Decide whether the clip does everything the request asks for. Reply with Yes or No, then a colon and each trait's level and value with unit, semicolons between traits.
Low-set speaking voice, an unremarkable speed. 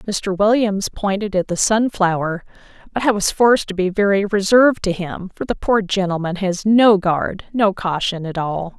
No: high, 195 Hz; average, 185 wpm